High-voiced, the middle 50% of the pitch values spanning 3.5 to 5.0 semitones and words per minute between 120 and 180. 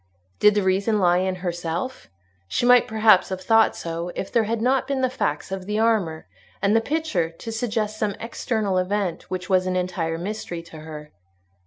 No: high, 195 Hz; average, 4.1 semitones; average, 190 wpm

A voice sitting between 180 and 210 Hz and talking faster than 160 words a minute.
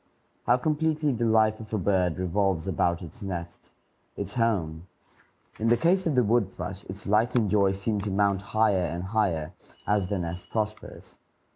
No: low, 100 Hz; average, 175 wpm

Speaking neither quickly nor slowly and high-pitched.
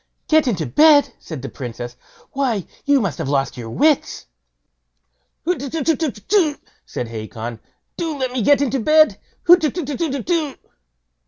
No: slow, 120 wpm; very high, 275 Hz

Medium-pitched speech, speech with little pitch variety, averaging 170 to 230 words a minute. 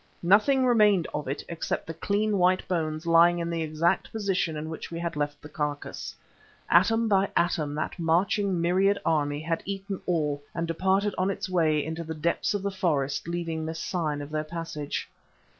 No: medium, 170 Hz; average, 3.5 semitones; average, 185 wpm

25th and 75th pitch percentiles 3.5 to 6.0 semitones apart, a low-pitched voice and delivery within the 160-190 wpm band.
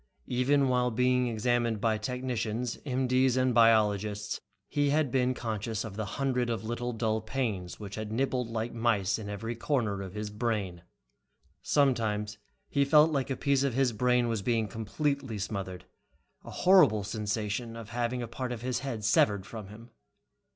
No: average, 3.0 semitones; low, 115 Hz; average, 165 wpm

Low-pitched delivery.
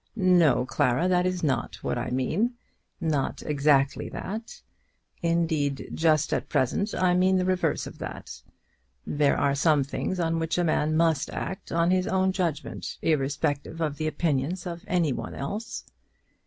No: medium, 165 Hz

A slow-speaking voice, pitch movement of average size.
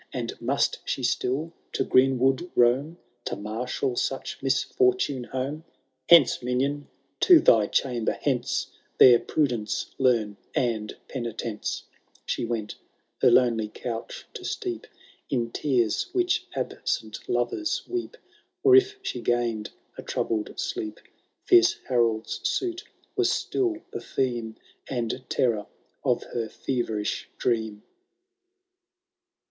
No: slow, 120 wpm; wide, 6.2 semitones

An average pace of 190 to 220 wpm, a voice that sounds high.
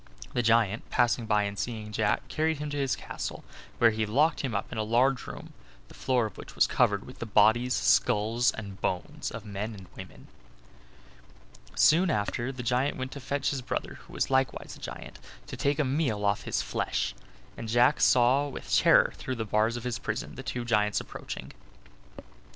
No: average, 195 wpm; low, 120 Hz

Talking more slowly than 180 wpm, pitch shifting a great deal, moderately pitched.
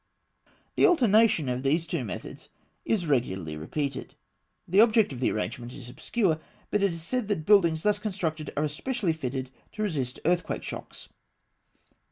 Yes: average, 155 wpm; wide, 7.8 semitones; medium, 160 Hz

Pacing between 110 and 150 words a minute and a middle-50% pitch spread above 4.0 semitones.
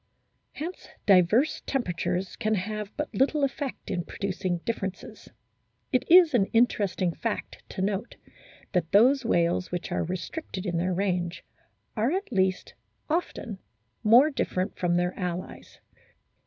Yes: slow, 135 wpm; wide, 5.5 semitones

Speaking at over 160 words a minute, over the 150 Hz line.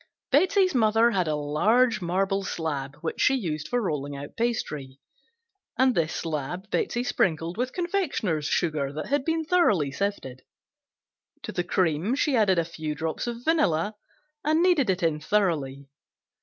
No: average, 155 wpm; medium, 185 Hz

